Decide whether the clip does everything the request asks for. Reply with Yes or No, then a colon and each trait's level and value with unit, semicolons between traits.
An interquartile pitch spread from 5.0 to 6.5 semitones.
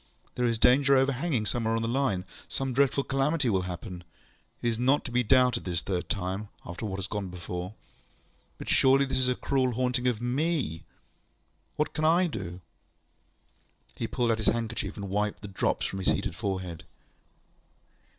Yes: wide, 5.5 semitones